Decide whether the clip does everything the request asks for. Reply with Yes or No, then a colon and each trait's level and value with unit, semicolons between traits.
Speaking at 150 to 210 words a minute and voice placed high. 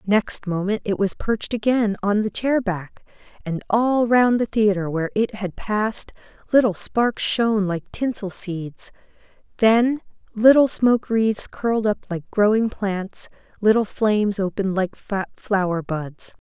No: average, 140 wpm; high, 210 Hz